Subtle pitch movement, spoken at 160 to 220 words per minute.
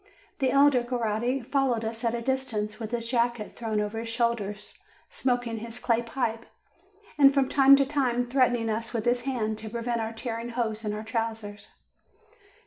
Yes: narrow, 2.0 semitones; average, 175 wpm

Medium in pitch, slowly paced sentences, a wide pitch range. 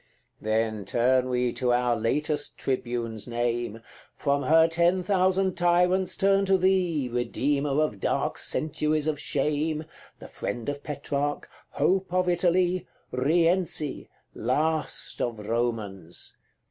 Yes: medium, 145 Hz; slow, 120 wpm; wide, 6.2 semitones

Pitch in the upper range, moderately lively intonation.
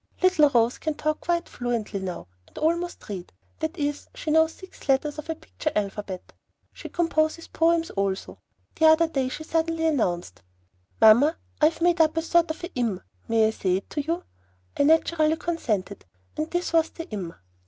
No: very high, 310 Hz; wide, 6.5 semitones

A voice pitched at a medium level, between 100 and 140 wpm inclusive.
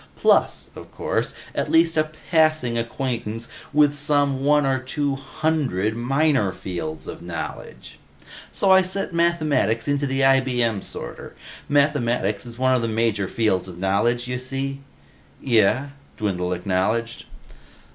No: low, 130 Hz; slow, 135 wpm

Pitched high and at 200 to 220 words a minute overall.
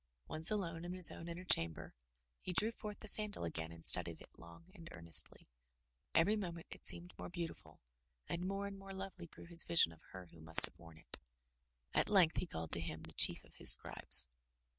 No: medium, 170 Hz; fast, 205 wpm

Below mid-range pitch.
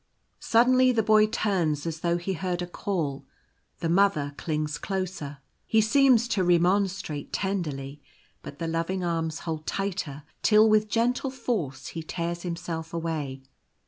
No: medium, 175 Hz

